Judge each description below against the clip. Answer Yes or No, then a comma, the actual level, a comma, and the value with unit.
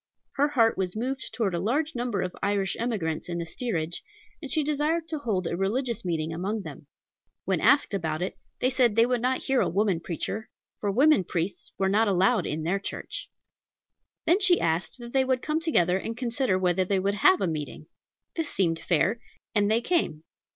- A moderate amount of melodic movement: No, wide, 6.3 semitones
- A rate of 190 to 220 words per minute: Yes, average, 200 wpm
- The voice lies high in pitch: Yes, high, 210 Hz